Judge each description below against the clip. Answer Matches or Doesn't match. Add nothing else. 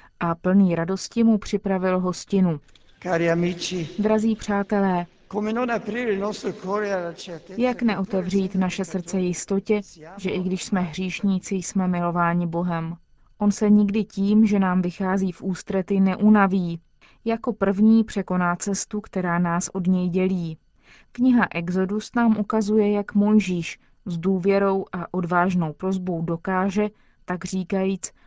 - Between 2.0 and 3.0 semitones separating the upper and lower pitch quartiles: Matches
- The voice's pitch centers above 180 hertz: Matches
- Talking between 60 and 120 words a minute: Matches